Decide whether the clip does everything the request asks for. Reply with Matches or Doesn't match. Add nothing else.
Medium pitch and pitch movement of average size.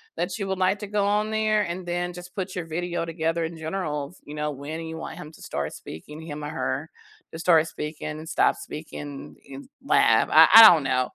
Matches